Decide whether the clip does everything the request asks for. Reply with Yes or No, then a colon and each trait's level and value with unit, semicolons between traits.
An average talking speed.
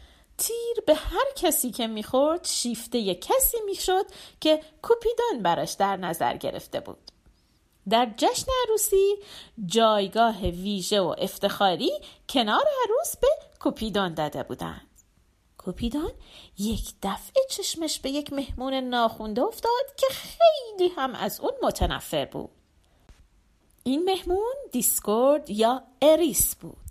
Yes: average, 115 wpm